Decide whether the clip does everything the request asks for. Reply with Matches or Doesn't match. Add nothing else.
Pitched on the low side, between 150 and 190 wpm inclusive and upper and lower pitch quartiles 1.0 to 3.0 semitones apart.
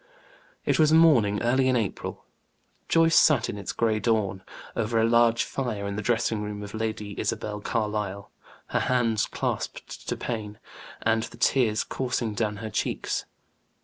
Matches